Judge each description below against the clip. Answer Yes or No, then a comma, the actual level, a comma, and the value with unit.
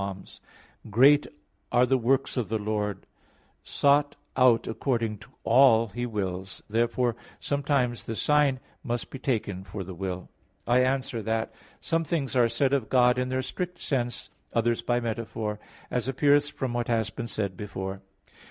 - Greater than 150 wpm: Yes, average, 160 wpm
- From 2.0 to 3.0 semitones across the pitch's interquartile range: No, average, 3.6 semitones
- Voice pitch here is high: No, low, 120 Hz